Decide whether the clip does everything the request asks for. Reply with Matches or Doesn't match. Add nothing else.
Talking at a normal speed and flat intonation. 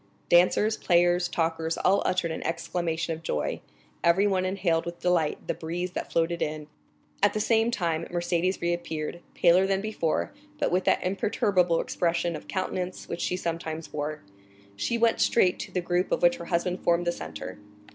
Matches